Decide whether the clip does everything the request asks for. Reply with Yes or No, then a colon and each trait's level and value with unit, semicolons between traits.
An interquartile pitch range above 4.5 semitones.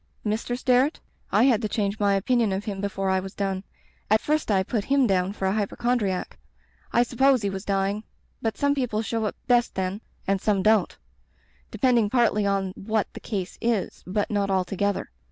No: average, 3.4 semitones